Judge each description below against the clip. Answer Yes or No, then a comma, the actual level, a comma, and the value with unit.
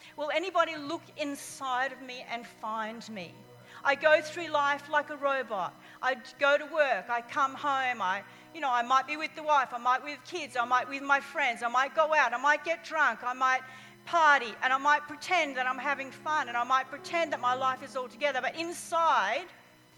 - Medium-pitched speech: No, very high, 280 Hz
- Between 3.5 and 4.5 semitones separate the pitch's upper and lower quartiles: No, average, 3.1 semitones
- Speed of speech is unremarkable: No, fast, 220 wpm